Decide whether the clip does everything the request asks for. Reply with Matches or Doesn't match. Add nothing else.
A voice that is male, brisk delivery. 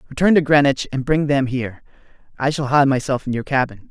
Matches